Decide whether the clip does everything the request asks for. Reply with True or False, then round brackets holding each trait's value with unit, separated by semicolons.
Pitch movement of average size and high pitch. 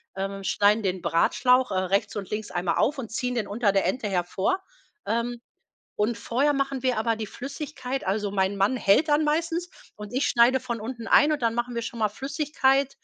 True (4.7 semitones; 235 Hz)